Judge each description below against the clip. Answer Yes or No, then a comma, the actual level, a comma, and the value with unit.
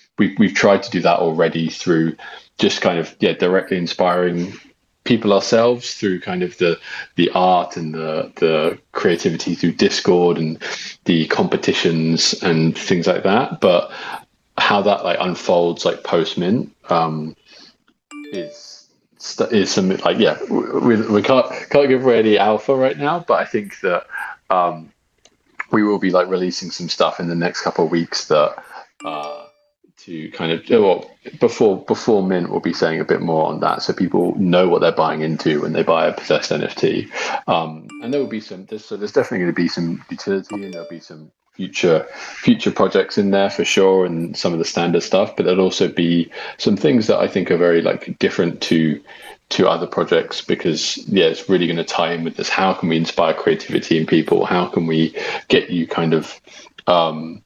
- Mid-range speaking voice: No, very low, 85 Hz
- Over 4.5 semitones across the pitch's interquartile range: No, average, 3.2 semitones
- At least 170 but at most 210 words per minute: Yes, average, 190 wpm